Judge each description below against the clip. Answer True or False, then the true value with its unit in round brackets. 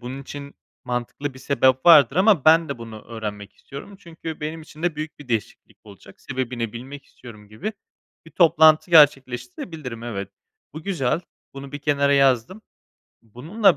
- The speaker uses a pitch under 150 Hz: True (140 Hz)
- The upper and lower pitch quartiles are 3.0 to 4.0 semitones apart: False (4.7 semitones)